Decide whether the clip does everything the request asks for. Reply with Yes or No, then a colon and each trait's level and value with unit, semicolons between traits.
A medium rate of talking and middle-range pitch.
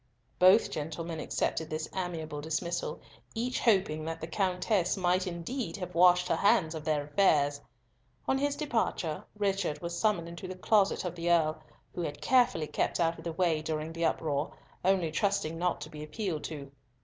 Yes: average, 175 wpm; medium, 170 Hz